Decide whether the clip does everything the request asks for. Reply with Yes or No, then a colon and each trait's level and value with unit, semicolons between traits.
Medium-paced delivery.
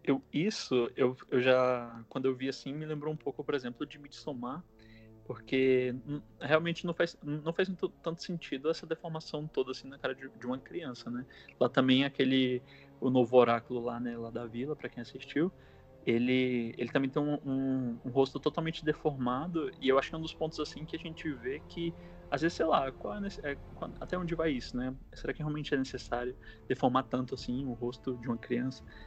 No: fast, 210 wpm